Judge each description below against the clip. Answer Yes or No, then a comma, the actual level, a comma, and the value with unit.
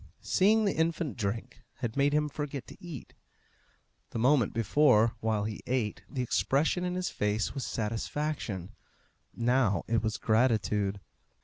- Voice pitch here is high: No, low, 120 Hz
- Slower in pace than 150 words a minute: Yes, average, 140 wpm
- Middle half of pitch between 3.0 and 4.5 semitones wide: No, wide, 5.4 semitones